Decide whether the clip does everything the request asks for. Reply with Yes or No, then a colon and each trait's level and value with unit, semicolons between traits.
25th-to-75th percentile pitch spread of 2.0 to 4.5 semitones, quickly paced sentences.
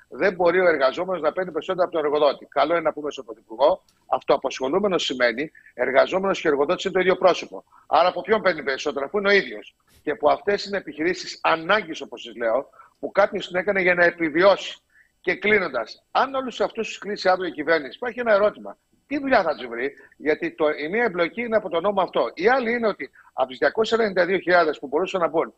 No: average, 5.0 semitones; fast, 210 wpm